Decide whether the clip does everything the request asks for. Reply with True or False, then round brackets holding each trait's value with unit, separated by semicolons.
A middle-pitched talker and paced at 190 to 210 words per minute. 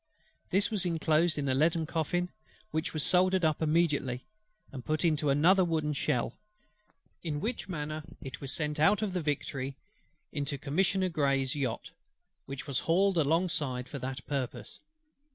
False (155 Hz; 155 wpm)